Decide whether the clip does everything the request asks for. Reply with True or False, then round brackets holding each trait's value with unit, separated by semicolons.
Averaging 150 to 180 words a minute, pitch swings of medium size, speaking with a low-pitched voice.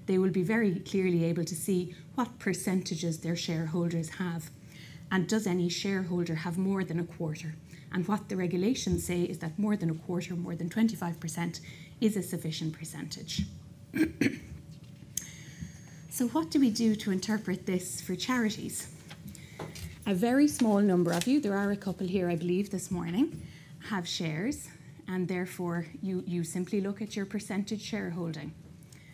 False (160 wpm; 3.1 semitones; 180 Hz)